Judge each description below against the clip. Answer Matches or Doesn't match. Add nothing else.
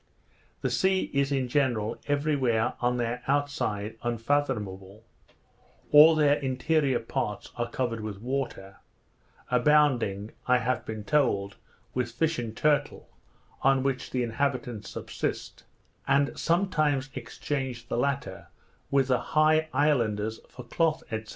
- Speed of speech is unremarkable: Doesn't match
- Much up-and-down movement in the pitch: Doesn't match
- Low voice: Matches